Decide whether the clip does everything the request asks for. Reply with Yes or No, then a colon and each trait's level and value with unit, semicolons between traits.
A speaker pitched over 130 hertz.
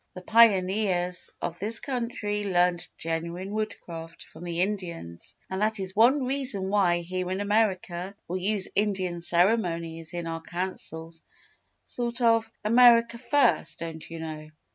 Yes: medium, 185 Hz